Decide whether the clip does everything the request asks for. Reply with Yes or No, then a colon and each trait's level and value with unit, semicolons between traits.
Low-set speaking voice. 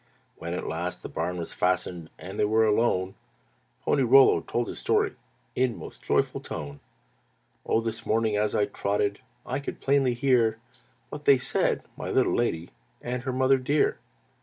Yes: low, 110 Hz